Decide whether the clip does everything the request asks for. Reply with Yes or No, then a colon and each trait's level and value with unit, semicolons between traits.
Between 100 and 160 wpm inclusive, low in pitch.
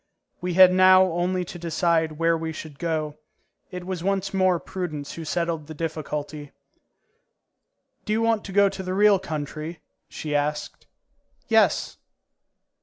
No: average, 145 wpm; medium, 170 Hz